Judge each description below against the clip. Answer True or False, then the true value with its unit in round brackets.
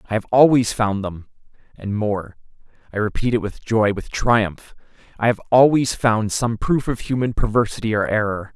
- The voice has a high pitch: False (110 Hz)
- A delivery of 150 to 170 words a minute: True (160 wpm)